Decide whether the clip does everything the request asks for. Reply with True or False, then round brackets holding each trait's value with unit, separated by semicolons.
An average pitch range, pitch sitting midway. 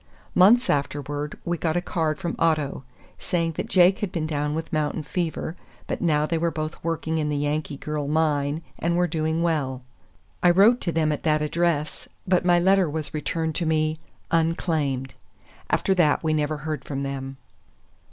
False (2.3 semitones; 155 Hz)